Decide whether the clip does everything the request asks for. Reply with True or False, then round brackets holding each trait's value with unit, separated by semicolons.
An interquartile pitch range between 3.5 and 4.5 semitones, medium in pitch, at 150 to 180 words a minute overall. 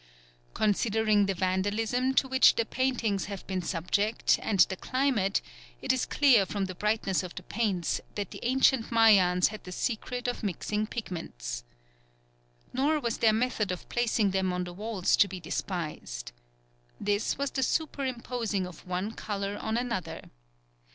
False (4.2 semitones; 210 Hz; 155 wpm)